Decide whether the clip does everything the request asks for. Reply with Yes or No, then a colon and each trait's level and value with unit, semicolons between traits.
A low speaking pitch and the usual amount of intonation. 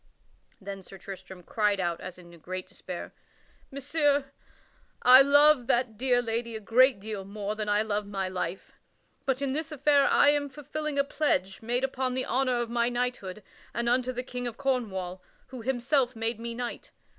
No: high, 240 Hz; average, 4.6 semitones